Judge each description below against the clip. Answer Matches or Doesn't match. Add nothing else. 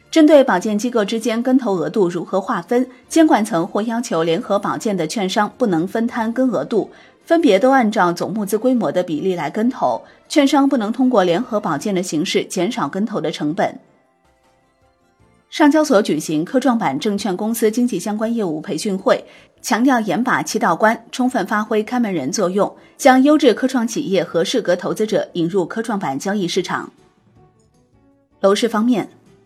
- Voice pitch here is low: Doesn't match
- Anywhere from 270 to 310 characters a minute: Matches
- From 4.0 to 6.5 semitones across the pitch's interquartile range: Matches